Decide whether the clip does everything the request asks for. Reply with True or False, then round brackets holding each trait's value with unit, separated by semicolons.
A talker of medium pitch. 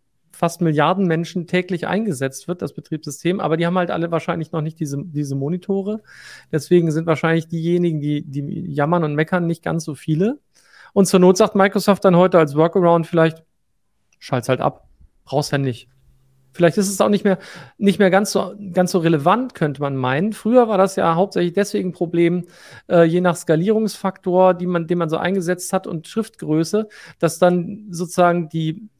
True (175 Hz)